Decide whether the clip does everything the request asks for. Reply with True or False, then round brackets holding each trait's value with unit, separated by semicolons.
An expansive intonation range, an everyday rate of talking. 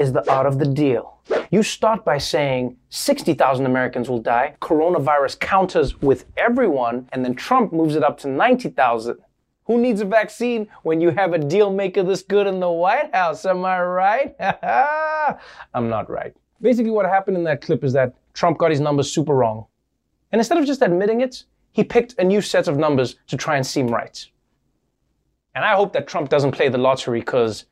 True (7.9 semitones; 195 wpm)